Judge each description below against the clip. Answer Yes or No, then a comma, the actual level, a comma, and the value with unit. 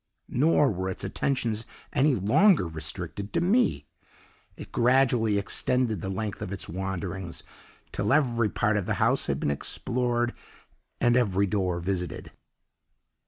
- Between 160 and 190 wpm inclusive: No, slow, 135 wpm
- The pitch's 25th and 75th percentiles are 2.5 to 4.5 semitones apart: No, average, 4.9 semitones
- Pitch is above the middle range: No, low, 105 Hz